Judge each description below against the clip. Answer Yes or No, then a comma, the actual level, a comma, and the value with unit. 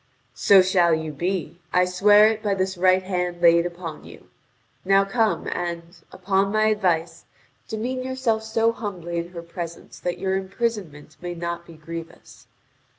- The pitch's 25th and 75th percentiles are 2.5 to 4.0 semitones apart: Yes, average, 3.2 semitones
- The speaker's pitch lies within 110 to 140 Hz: No, medium, 185 Hz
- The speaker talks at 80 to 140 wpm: No, average, 155 wpm